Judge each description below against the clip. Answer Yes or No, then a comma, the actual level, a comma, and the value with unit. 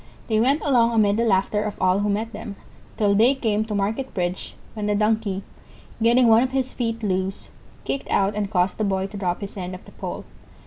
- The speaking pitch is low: No, high, 210 Hz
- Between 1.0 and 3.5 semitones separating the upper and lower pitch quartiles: Yes, average, 2.7 semitones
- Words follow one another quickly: Yes, fast, 220 wpm